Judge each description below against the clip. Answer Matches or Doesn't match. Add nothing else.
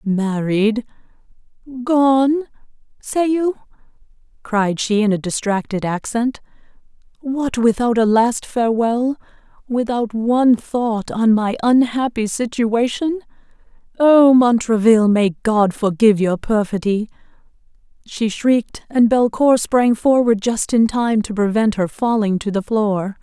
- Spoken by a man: Doesn't match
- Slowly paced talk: Matches